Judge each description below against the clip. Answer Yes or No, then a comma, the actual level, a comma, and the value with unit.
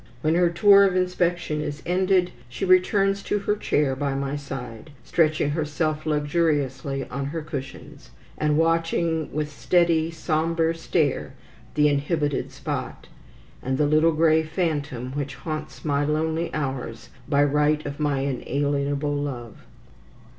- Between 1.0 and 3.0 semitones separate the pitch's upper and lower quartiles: Yes, average, 2.7 semitones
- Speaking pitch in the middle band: Yes, medium, 150 Hz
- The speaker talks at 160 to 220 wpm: No, slow, 135 wpm